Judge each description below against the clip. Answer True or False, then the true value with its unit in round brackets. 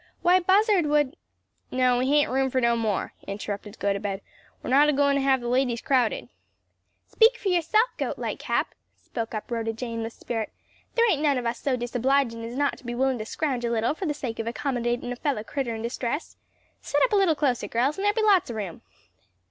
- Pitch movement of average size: True (4.2 semitones)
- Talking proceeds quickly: True (215 wpm)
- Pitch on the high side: True (255 Hz)